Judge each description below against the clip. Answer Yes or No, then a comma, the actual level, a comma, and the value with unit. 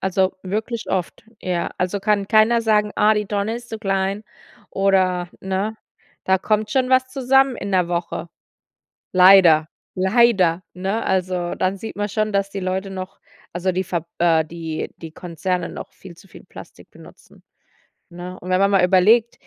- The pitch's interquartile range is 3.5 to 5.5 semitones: No, average, 2.7 semitones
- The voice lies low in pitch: No, high, 190 Hz